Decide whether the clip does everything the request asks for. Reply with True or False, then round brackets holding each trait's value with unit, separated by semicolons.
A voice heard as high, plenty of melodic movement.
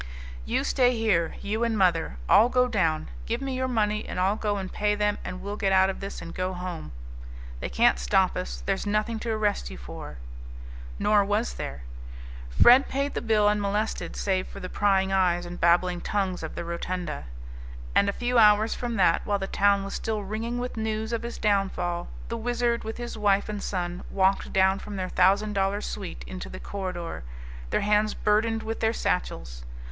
False (200 Hz; 3.2 semitones)